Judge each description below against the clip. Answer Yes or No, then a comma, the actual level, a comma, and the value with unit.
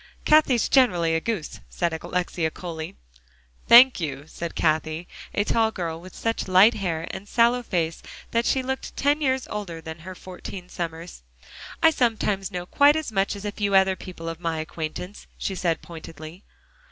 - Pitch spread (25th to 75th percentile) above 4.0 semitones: Yes, wide, 5.5 semitones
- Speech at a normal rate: Yes, average, 170 wpm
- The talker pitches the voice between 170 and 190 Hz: Yes, medium, 185 Hz